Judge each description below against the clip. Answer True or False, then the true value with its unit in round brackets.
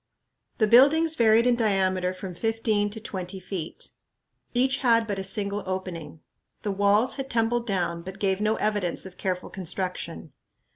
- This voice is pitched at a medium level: False (200 Hz)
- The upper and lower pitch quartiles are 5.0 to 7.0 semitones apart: False (3.4 semitones)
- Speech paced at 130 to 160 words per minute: True (155 wpm)